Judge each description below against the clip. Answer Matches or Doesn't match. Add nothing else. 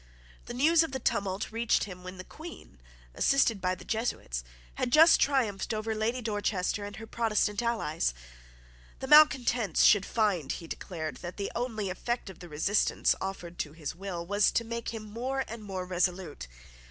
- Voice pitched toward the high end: Matches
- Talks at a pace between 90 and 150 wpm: Doesn't match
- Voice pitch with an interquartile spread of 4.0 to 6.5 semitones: Matches